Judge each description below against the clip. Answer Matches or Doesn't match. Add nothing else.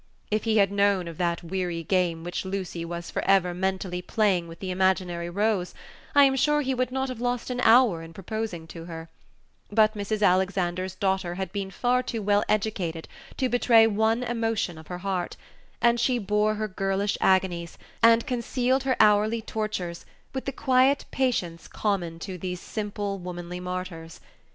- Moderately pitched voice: Doesn't match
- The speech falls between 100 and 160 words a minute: Doesn't match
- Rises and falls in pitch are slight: Doesn't match